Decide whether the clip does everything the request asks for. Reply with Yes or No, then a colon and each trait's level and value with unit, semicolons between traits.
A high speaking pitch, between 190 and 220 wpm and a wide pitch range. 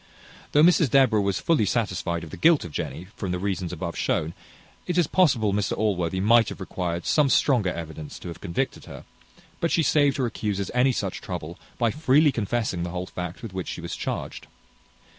No: low, 100 Hz; average, 200 wpm; wide, 6.7 semitones